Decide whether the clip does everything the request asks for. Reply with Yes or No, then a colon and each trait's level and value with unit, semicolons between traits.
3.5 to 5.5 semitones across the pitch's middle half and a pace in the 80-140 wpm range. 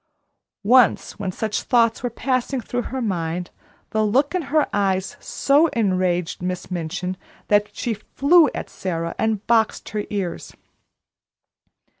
Yes: average, 5.2 semitones; slow, 135 wpm